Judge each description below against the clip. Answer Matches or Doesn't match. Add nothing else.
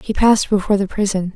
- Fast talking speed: Matches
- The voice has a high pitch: Matches